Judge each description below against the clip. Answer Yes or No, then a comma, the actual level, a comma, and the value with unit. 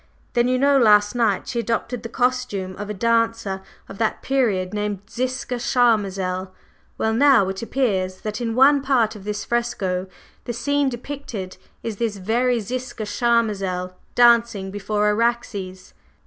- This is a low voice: No, high, 230 Hz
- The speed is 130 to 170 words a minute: Yes, average, 150 wpm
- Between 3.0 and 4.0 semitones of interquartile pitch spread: Yes, average, 3.6 semitones